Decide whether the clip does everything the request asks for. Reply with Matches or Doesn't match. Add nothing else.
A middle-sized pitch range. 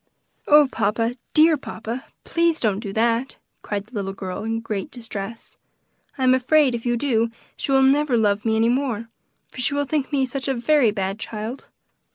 Matches